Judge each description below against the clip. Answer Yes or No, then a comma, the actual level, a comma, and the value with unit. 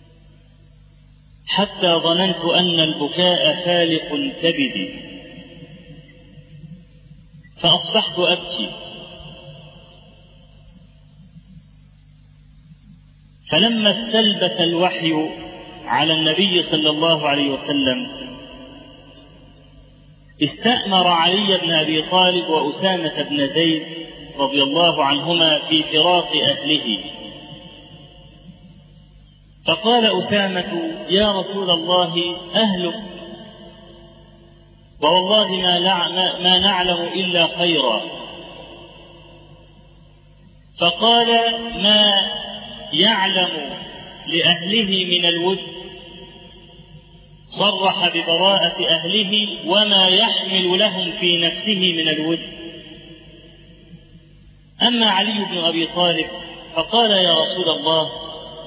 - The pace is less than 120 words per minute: Yes, average, 70 wpm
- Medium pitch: Yes, medium, 170 Hz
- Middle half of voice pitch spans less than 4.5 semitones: Yes, narrow, 2.5 semitones